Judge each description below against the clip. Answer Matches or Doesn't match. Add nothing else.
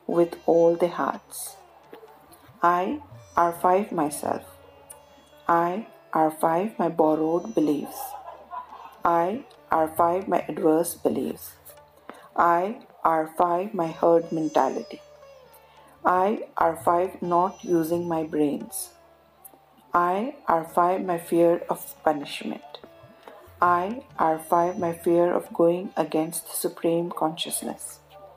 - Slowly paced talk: Matches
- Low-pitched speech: Doesn't match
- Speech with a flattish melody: Matches